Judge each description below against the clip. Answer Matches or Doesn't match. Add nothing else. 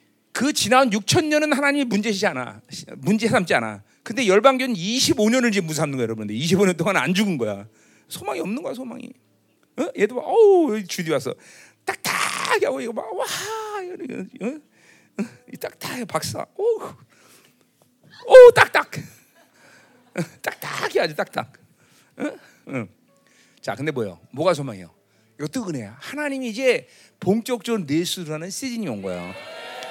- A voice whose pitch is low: Doesn't match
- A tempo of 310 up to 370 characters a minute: Doesn't match